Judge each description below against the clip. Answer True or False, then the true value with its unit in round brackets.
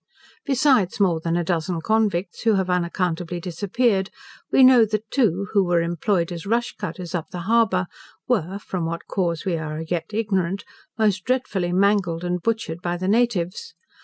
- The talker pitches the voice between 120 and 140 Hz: False (185 Hz)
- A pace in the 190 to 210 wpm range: False (165 wpm)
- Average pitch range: True (3.9 semitones)